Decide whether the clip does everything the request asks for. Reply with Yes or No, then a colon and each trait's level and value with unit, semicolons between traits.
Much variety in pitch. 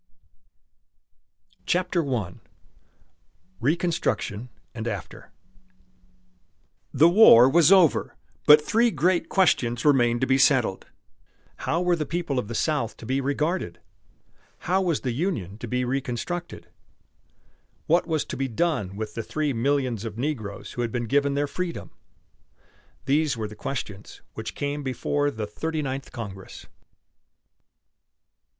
Yes: wide, 5.7 semitones